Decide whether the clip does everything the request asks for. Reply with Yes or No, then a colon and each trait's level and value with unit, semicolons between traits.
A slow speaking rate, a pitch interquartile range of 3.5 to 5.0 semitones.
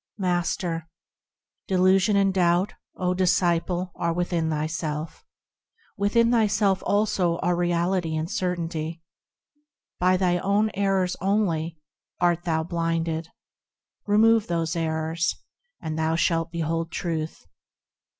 No: slow, 105 wpm; narrow, 2.6 semitones